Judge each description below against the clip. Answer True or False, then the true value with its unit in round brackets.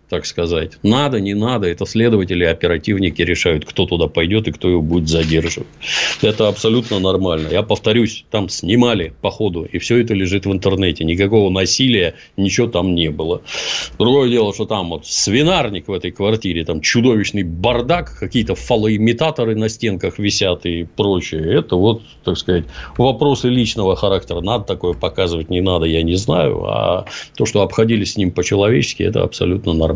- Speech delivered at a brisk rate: True (165 wpm)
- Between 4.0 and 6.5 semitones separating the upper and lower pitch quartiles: True (4.3 semitones)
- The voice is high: False (100 Hz)